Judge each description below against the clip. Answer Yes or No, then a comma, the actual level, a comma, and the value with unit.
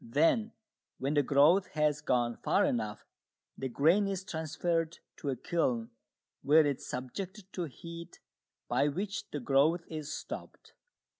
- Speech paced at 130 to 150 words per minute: Yes, average, 145 wpm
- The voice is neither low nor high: Yes, medium, 155 Hz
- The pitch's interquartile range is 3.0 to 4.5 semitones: Yes, average, 4.1 semitones